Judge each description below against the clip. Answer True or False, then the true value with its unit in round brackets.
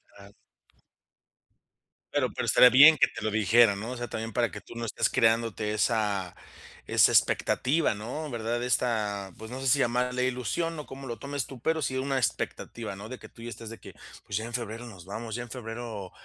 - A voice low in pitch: True (115 Hz)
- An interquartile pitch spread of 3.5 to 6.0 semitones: False (2.7 semitones)